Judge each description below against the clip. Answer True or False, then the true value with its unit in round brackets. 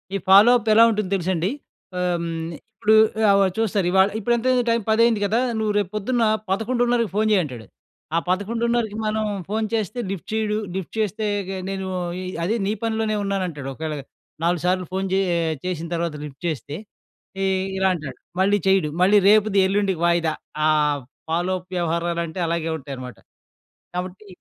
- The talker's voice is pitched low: False (190 Hz)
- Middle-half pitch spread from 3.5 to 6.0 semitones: True (4.1 semitones)